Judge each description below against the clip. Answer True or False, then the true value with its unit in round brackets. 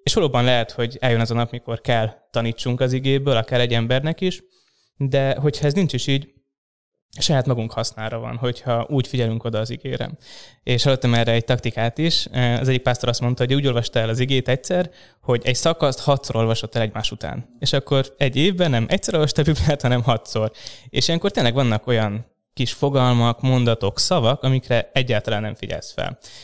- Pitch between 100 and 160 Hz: True (125 Hz)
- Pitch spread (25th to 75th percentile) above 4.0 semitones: False (3.0 semitones)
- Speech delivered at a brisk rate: True (190 wpm)